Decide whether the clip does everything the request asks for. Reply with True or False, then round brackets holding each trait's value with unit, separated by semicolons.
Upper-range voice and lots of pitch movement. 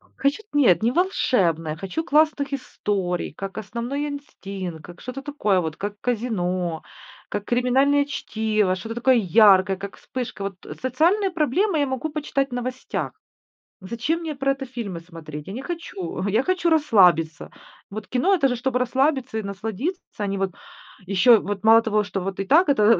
True (230 Hz; 6.3 semitones)